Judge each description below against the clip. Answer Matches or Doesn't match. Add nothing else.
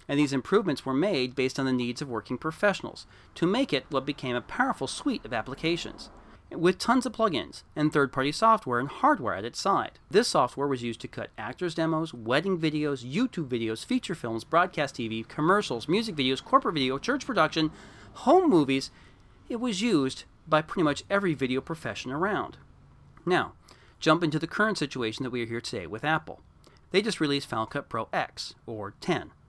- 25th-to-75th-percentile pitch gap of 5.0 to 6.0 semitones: Matches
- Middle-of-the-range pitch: Matches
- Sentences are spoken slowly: Doesn't match